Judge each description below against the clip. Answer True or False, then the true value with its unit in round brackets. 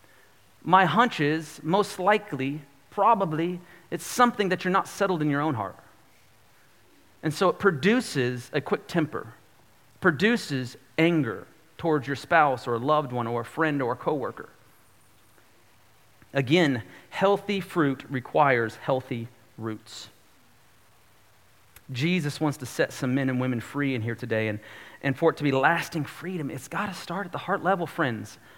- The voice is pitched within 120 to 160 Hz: True (140 Hz)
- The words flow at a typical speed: True (155 wpm)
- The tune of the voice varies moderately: False (6.4 semitones)